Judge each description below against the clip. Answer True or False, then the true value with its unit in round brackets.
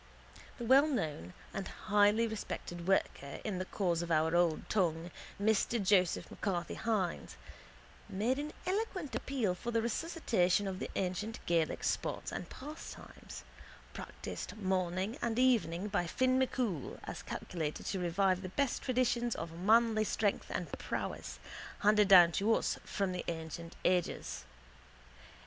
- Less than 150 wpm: True (135 wpm)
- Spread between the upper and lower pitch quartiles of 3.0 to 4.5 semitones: False (4.9 semitones)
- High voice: True (195 Hz)